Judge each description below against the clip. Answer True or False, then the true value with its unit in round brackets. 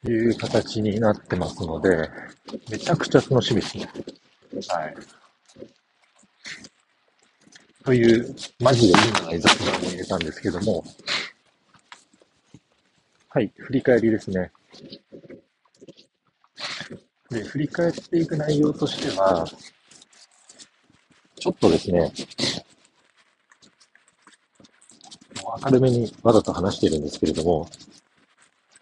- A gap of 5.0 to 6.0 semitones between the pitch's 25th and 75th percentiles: False (4.2 semitones)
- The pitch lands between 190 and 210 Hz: False (115 Hz)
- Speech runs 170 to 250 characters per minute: True (200 characters per minute)